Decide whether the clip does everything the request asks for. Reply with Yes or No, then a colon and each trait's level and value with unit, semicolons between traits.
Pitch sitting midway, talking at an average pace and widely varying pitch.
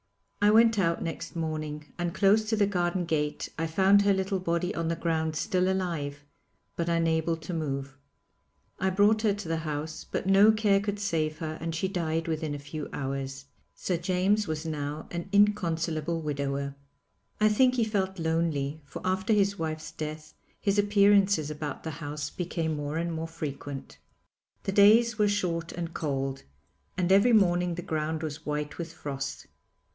No: medium, 165 Hz; average, 170 wpm; average, 4.1 semitones